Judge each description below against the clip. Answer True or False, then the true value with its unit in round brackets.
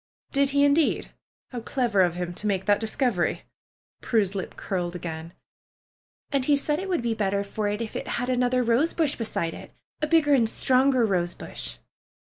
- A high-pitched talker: True (230 Hz)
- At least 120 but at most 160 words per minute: False (185 wpm)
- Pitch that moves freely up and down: True (6.2 semitones)